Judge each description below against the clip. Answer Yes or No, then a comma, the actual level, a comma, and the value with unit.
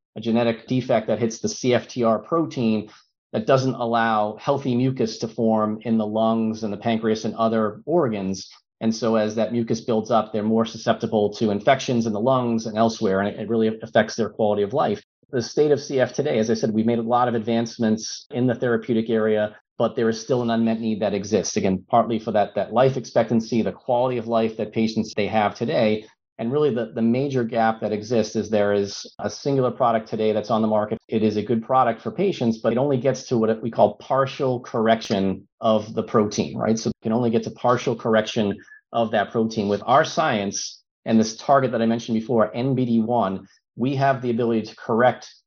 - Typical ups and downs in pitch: No, narrow, 1.8 semitones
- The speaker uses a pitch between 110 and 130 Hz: Yes, low, 115 Hz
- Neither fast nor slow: No, fast, 210 wpm